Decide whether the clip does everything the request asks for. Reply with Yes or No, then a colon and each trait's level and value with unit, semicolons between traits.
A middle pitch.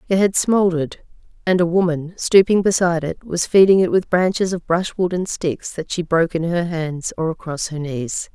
Yes: medium, 175 Hz